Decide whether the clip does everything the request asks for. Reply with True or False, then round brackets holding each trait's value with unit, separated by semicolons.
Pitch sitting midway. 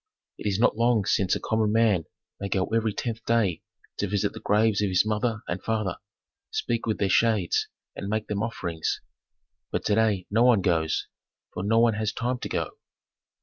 False (105 Hz)